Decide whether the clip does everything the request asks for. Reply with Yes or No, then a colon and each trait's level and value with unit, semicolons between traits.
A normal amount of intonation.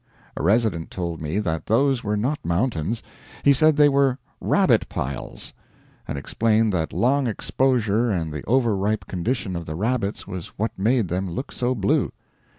No: wide, 6.2 semitones